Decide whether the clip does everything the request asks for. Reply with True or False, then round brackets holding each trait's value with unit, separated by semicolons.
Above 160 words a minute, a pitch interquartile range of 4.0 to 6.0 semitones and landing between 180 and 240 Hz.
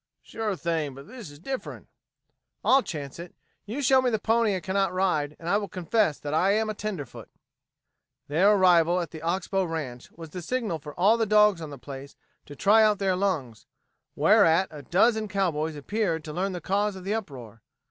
True (200 wpm; 5.3 semitones; 185 Hz)